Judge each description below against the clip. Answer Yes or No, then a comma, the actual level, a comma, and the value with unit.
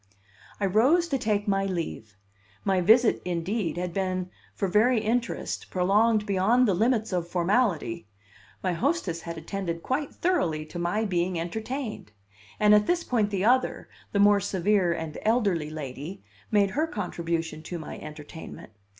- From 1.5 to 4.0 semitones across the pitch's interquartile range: No, average, 4.4 semitones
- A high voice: Yes, high, 195 Hz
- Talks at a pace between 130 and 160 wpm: Yes, average, 150 wpm